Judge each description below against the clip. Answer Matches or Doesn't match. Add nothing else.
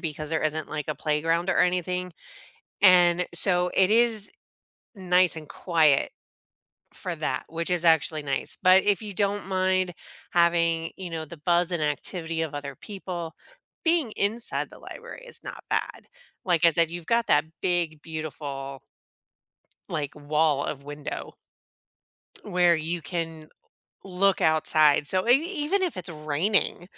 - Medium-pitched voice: Matches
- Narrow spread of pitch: Doesn't match